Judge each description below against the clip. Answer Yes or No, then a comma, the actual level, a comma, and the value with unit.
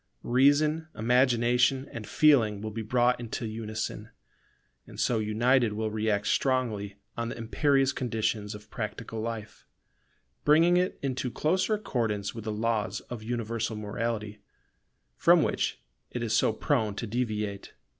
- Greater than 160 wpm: No, slow, 135 wpm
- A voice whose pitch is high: No, low, 115 Hz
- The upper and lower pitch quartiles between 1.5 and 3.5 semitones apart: Yes, average, 3.0 semitones